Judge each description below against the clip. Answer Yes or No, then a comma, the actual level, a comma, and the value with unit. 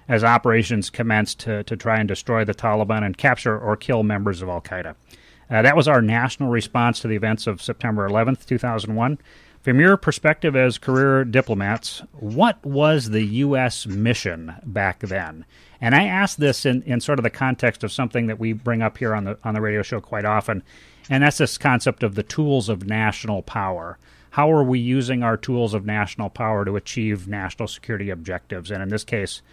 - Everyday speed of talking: Yes, average, 195 wpm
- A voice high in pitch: No, low, 110 Hz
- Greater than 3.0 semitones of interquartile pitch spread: Yes, average, 3.7 semitones